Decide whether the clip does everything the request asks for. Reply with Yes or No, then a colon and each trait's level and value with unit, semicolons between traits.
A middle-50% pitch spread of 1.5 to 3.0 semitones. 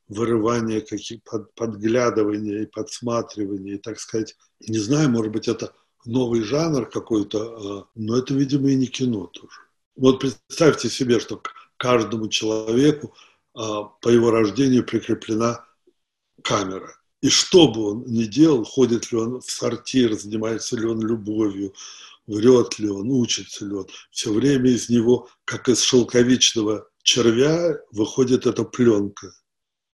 Yes: narrow, 2.6 semitones